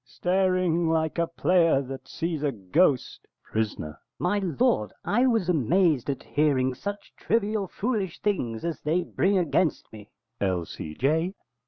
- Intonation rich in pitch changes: Yes, wide, 5.8 semitones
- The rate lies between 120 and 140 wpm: Yes, slow, 135 wpm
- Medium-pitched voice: Yes, medium, 165 Hz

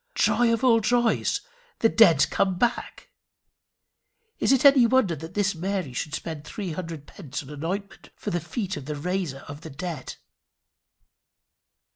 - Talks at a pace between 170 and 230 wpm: No, average, 160 wpm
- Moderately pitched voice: Yes, medium, 180 Hz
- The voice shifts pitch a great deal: Yes, wide, 6.5 semitones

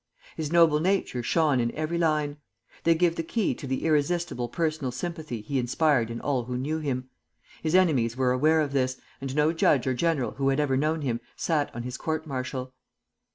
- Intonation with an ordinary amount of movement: Yes, average, 3.8 semitones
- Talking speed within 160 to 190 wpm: No, average, 200 wpm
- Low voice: No, medium, 145 Hz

